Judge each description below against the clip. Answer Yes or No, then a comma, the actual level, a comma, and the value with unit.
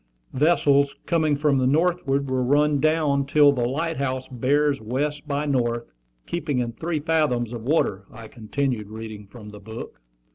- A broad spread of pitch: No, average, 3.9 semitones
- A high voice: No, medium, 140 Hz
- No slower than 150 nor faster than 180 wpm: Yes, average, 160 wpm